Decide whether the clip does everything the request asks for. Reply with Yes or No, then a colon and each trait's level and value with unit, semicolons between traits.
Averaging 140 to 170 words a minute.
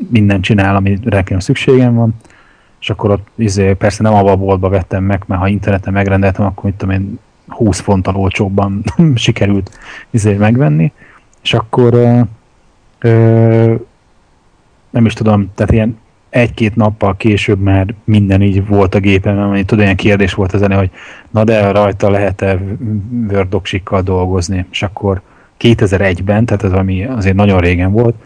Yes: average, 150 wpm